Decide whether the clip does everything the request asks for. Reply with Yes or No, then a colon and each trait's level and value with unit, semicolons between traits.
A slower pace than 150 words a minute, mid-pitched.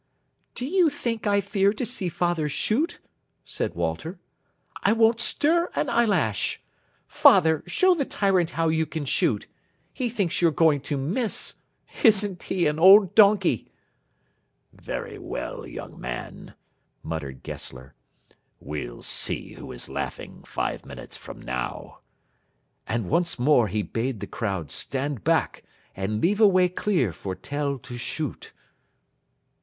Yes: average, 140 wpm; medium, 165 Hz